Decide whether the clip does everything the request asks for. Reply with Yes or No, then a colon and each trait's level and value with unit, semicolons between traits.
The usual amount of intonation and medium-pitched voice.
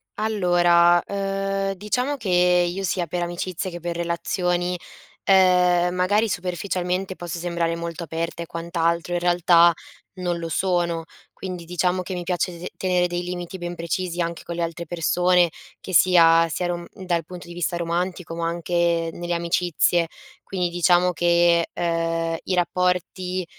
No: narrow, 1.2 semitones; medium, 175 Hz